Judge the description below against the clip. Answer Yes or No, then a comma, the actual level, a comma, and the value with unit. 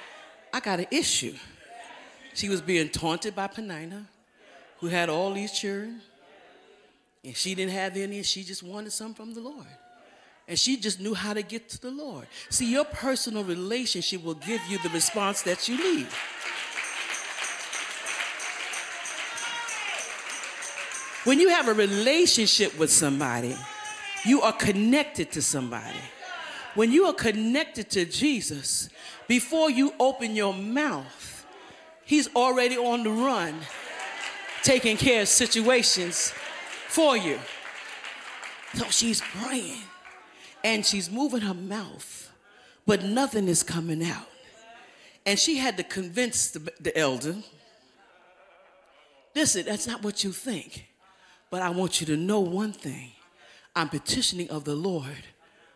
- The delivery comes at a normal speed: No, slow, 130 wpm